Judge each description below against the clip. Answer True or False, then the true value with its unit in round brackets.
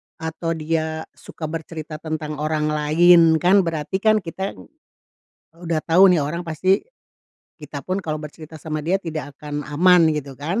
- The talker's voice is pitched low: False (160 Hz)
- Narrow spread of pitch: True (2.3 semitones)